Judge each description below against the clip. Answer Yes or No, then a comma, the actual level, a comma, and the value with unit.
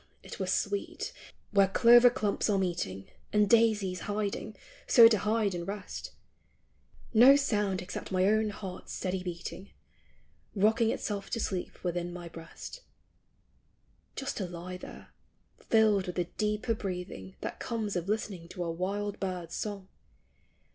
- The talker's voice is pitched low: No, high, 200 Hz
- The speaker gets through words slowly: No, average, 145 wpm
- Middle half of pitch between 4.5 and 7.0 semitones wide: No, average, 3.0 semitones